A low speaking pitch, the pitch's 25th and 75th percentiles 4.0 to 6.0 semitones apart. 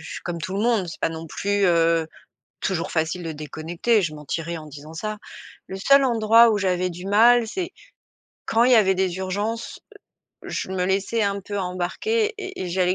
No: high, 190 Hz; average, 4.6 semitones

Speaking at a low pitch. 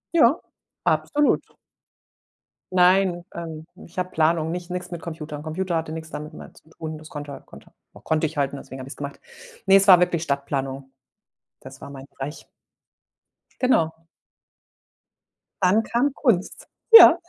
No: medium, 160 Hz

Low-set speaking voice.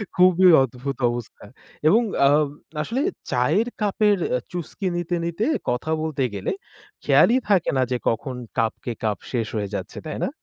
No: medium, 155 Hz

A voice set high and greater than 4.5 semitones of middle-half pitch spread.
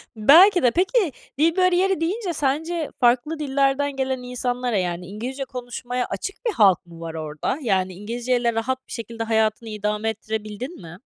Yes: high, 245 Hz; average, 5.2 semitones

